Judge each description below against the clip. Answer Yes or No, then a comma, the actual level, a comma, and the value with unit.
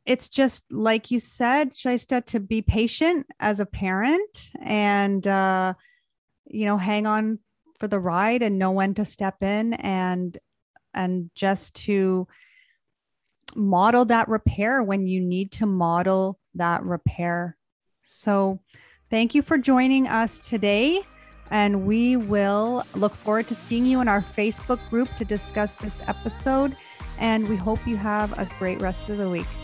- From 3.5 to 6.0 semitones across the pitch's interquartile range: Yes, average, 3.8 semitones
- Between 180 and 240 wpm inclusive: No, average, 150 wpm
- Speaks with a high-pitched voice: Yes, high, 210 Hz